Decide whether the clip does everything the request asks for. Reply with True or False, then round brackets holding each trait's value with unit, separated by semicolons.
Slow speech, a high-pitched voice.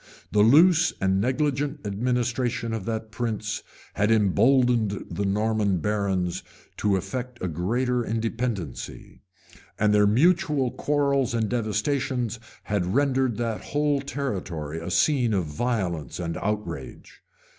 False (120 wpm; 115 Hz)